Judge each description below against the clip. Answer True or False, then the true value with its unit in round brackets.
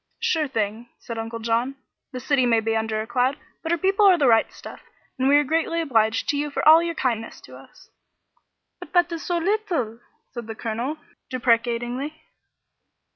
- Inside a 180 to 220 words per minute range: True (185 wpm)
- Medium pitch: False (255 Hz)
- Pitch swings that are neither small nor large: False (5.8 semitones)